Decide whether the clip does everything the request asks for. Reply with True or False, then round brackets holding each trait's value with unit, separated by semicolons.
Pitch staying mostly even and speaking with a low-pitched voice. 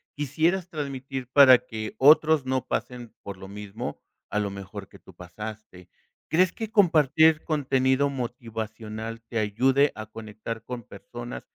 False (4.7 semitones; 120 Hz)